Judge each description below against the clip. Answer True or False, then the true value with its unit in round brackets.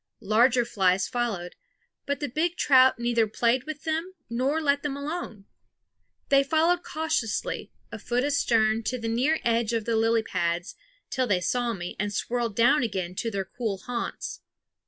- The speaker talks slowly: False (165 wpm)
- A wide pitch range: False (4.5 semitones)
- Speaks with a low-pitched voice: False (240 Hz)